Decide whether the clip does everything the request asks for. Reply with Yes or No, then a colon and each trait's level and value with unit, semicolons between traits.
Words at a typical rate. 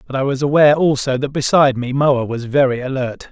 No: fast, 215 wpm